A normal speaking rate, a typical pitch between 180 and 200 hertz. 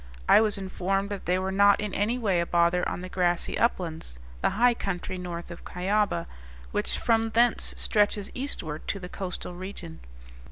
Yes: average, 175 wpm; high, 190 Hz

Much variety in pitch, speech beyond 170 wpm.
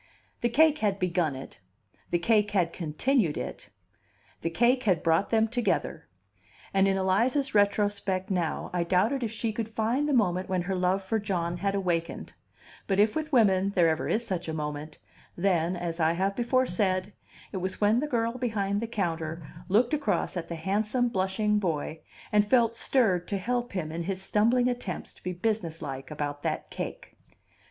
No: average, 4.5 semitones; average, 180 wpm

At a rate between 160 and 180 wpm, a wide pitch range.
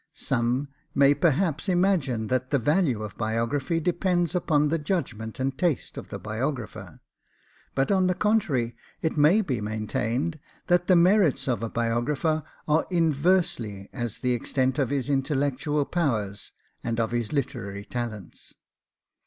No: average, 145 wpm; wide, 5.8 semitones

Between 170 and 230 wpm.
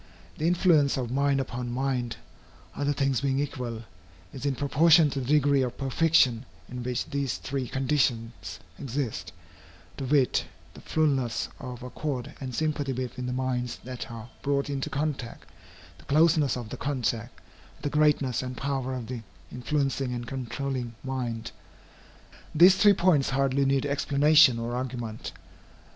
No: average, 150 wpm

